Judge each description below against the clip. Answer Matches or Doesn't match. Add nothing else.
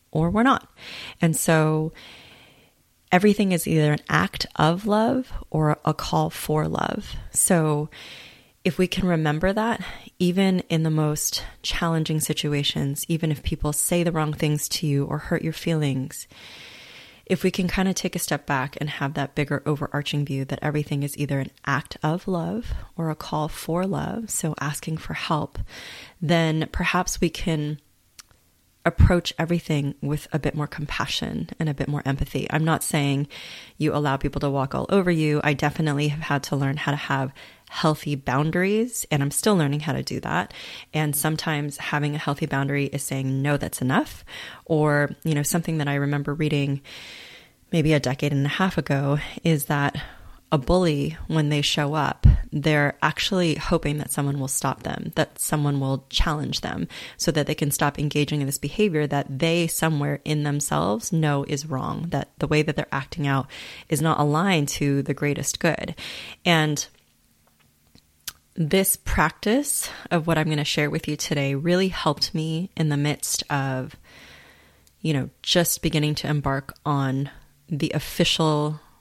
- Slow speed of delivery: Doesn't match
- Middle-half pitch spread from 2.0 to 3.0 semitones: Matches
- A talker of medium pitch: Matches